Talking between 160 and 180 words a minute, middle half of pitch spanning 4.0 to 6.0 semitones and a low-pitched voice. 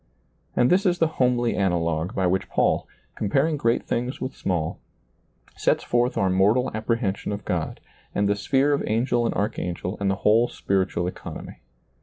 Yes: average, 165 wpm; average, 4.6 semitones; low, 110 Hz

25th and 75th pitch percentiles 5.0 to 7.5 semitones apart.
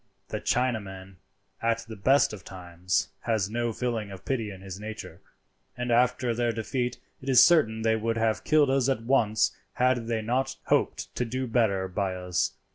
No: average, 3.6 semitones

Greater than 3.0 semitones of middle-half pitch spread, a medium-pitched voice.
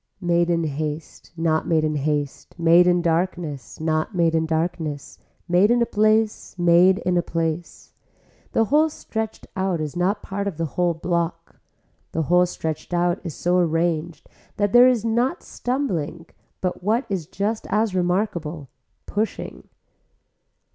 Yes: average, 3.7 semitones; medium, 175 Hz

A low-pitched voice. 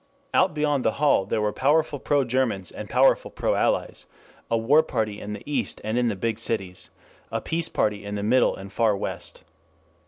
Yes: low, 115 Hz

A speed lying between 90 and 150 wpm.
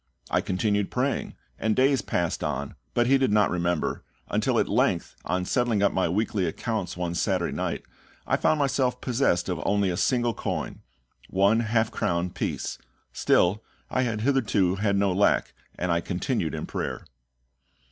No: average, 165 wpm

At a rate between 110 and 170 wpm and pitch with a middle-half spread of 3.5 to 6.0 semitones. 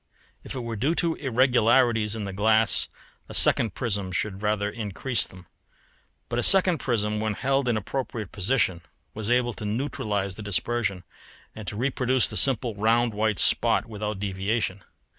No: average, 160 wpm; average, 3.0 semitones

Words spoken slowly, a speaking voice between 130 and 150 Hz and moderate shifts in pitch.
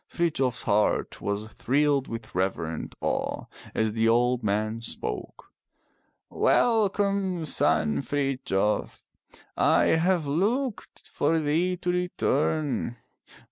No: slow, 100 wpm; medium, 140 Hz; wide, 8.1 semitones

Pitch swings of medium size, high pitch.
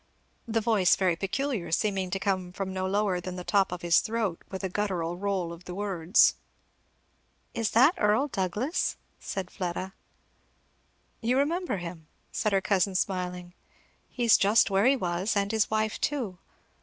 Yes: average, 3.2 semitones; high, 195 Hz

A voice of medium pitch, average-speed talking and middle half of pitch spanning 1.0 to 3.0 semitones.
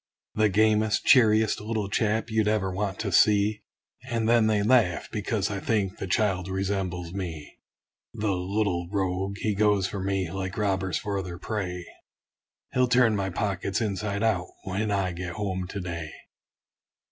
No: low, 100 Hz; average, 160 wpm; narrow, 2.4 semitones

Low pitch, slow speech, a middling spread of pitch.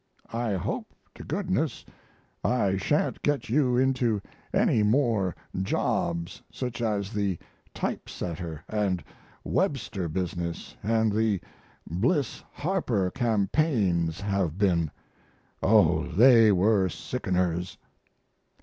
Yes: low, 100 Hz; slow, 100 wpm; average, 4.8 semitones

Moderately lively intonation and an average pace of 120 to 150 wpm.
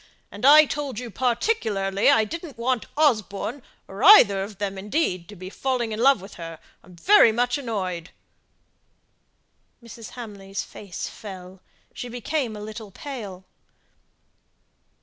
Yes: average, 4.8 semitones; slow, 135 wpm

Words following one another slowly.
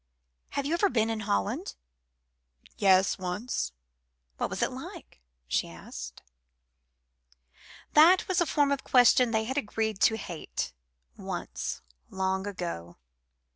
Yes: slow, 125 wpm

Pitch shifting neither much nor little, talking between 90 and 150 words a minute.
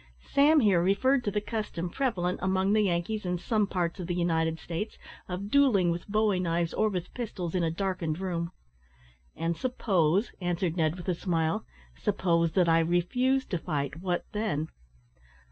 No: average, 3.7 semitones; average, 170 wpm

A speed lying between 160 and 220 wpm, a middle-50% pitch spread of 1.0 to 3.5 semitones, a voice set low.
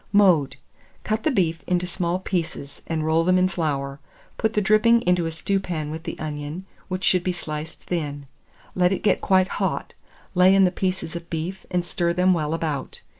No: average, 190 wpm; average, 2.8 semitones; medium, 175 Hz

